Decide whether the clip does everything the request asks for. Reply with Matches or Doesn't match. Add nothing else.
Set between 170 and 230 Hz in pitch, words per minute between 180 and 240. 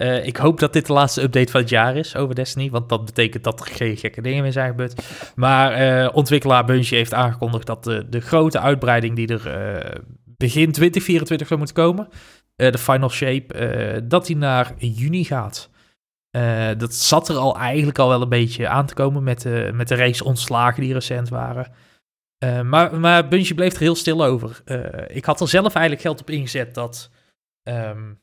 Doesn't match